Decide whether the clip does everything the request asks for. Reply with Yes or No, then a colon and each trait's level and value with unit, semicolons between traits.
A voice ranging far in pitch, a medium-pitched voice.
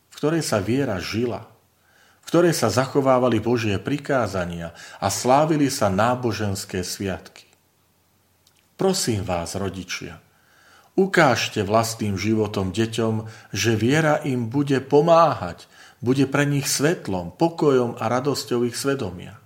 No: wide, 5.9 semitones; low, 115 Hz